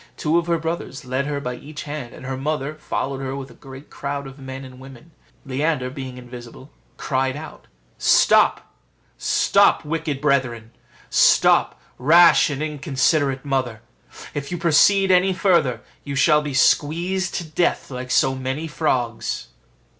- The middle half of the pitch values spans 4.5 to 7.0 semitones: No, average, 3.0 semitones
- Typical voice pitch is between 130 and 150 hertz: Yes, medium, 140 Hz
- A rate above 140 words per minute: Yes, average, 155 wpm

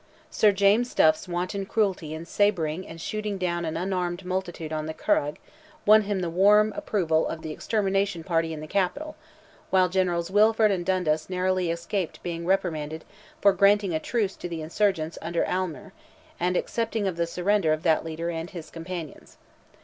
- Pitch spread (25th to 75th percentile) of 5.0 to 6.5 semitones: No, average, 3.3 semitones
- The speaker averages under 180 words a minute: Yes, average, 170 wpm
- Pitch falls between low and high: Yes, medium, 180 Hz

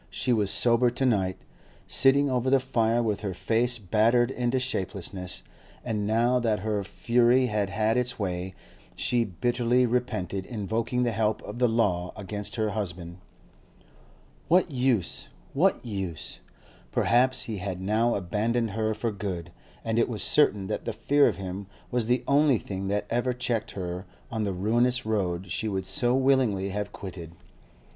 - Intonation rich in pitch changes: No, average, 3.9 semitones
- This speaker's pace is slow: No, average, 160 wpm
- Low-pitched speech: Yes, low, 110 Hz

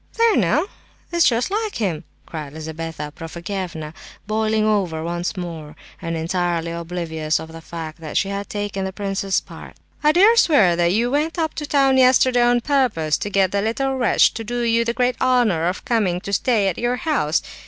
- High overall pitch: Yes, high, 200 Hz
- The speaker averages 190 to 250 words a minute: Yes, average, 195 wpm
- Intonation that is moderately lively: No, wide, 6.6 semitones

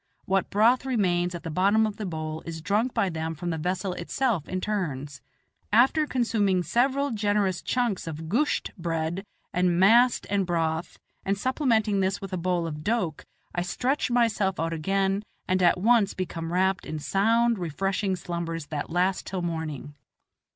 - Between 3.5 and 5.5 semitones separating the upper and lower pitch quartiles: Yes, average, 4.3 semitones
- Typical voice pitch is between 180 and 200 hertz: Yes, medium, 185 Hz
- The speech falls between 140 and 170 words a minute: Yes, average, 165 wpm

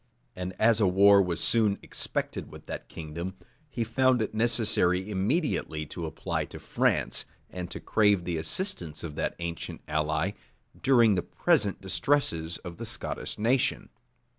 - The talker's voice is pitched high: No, very low, 95 Hz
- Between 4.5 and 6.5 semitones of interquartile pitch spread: Yes, average, 5.0 semitones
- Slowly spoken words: No, average, 150 wpm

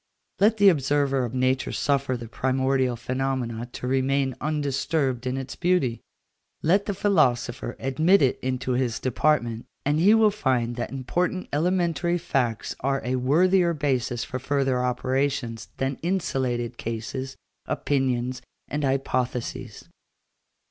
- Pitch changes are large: No, average, 3.2 semitones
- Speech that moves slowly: Yes, slow, 130 wpm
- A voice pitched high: No, low, 135 Hz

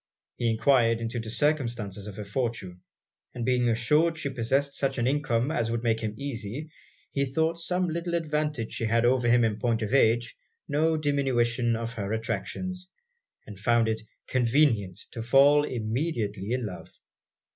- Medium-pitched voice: No, low, 120 Hz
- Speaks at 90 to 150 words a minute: No, average, 165 wpm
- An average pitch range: Yes, average, 4.2 semitones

